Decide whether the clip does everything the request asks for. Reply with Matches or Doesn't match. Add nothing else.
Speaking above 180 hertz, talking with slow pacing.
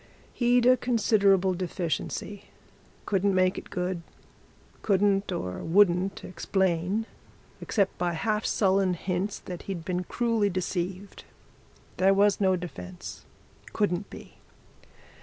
Matches